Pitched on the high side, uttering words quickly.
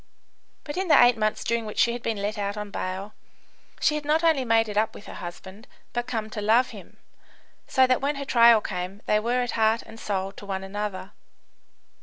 Yes: high, 220 Hz; fast, 215 wpm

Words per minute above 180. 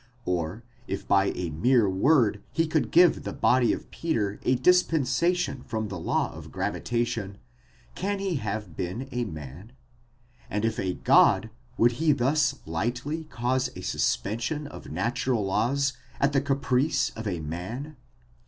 No: average, 155 wpm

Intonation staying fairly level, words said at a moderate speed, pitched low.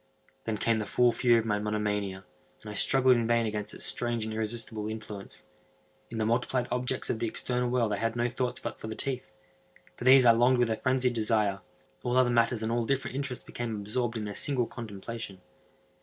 No: narrow, 2.3 semitones; fast, 210 wpm; low, 115 Hz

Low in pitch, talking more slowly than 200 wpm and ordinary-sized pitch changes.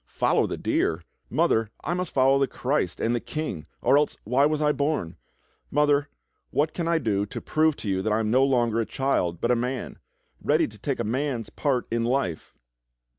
No: low, 130 Hz; fast, 205 wpm; average, 4.7 semitones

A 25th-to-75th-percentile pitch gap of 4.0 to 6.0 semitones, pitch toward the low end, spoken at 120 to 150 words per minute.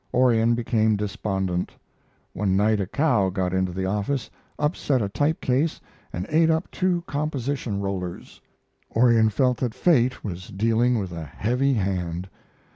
Yes: average, 5.2 semitones; low, 110 Hz; average, 140 wpm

